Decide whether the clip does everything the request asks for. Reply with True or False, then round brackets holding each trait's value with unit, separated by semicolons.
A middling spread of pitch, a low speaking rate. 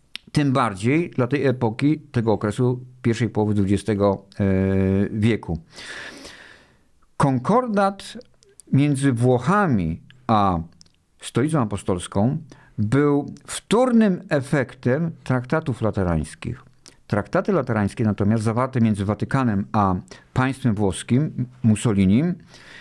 False (5.8 semitones; 85 wpm)